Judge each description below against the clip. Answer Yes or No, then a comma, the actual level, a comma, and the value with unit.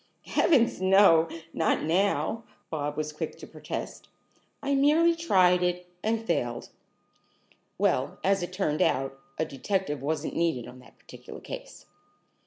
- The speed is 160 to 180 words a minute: No, slow, 135 wpm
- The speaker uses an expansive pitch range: Yes, wide, 6.4 semitones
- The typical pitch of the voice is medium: Yes, medium, 180 Hz